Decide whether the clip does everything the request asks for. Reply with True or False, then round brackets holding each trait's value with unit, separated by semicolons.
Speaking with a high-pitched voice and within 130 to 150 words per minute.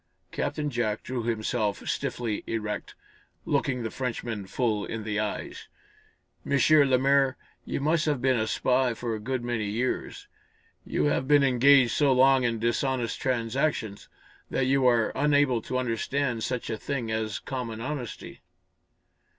False (125 Hz; 145 wpm)